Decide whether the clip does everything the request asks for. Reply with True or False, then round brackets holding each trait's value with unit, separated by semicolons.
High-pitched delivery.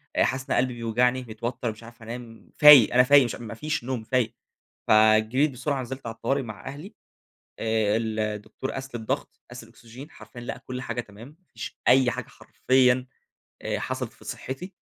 False (120 Hz)